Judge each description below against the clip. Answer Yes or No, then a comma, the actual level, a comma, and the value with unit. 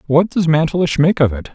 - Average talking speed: No, fast, 235 wpm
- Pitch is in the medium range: Yes, medium, 155 Hz